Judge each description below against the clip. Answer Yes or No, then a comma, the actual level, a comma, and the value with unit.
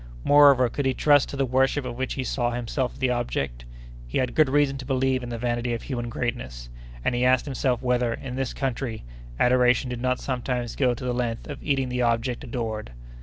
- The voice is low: Yes, low, 125 Hz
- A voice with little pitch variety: Yes, narrow, 1.8 semitones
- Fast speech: Yes, fast, 215 wpm